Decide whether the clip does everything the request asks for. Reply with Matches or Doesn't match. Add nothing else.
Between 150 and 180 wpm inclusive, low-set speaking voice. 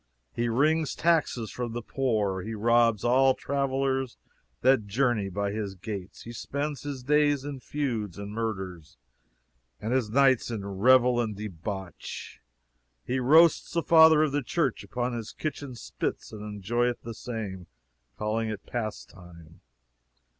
Doesn't match